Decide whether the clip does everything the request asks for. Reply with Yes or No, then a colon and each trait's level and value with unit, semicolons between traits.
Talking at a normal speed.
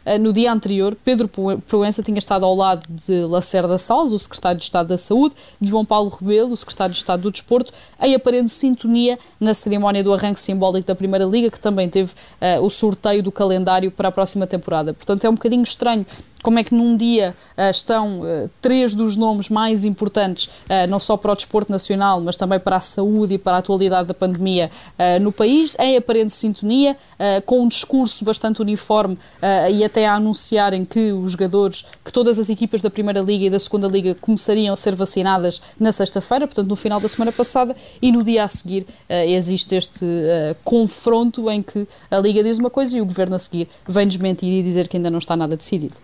No: fast, 210 wpm